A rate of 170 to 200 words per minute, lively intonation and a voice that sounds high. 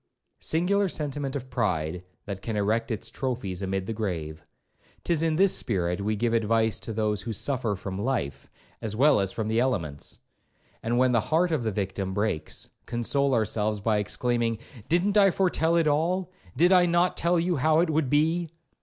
No: average, 180 wpm; wide, 7.4 semitones; low, 120 Hz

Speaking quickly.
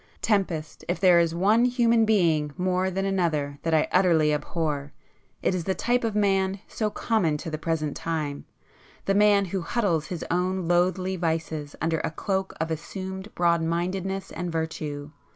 No: average, 170 wpm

